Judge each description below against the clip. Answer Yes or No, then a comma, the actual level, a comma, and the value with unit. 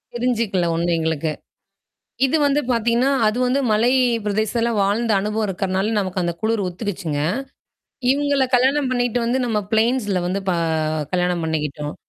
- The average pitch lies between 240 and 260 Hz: No, high, 215 Hz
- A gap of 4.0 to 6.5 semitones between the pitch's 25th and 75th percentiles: Yes, average, 5.2 semitones